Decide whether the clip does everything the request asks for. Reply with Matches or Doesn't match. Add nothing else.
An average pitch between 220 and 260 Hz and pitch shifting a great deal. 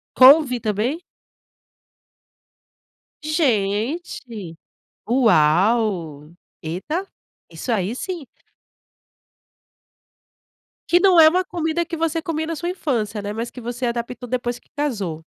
Matches